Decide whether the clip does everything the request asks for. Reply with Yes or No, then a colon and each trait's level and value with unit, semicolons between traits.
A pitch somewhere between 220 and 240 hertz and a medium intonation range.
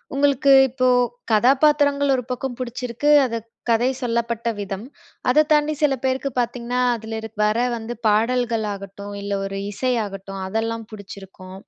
Yes: high, 235 Hz; average, 3.6 semitones